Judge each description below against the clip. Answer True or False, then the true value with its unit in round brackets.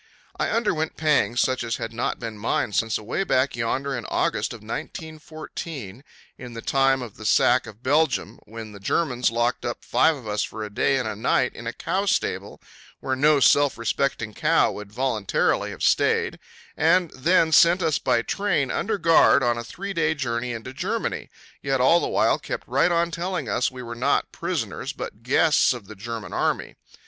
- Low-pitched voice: True (130 Hz)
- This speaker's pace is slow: False (190 wpm)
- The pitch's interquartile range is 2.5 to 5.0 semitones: False (5.4 semitones)